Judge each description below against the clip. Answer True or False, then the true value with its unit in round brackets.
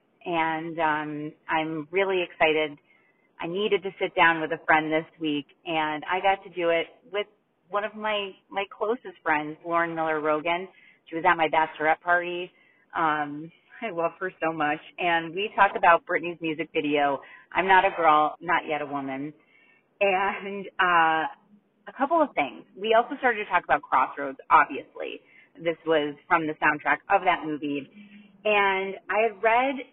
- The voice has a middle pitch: True (170 Hz)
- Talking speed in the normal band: True (170 wpm)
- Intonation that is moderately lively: True (4.1 semitones)